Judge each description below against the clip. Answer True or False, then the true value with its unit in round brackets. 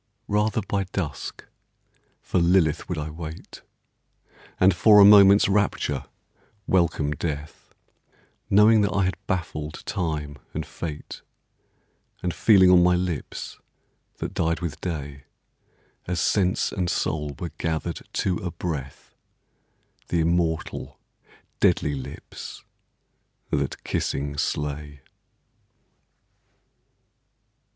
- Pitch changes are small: False (3.8 semitones)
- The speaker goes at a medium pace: False (105 wpm)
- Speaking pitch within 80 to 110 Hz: True (85 Hz)